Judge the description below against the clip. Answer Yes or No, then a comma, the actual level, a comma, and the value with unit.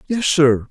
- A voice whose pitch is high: No, medium, 155 Hz